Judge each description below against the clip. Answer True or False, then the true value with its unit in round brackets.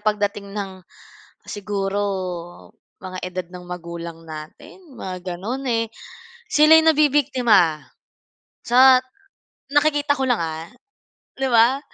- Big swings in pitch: True (6.7 semitones)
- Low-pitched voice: False (205 Hz)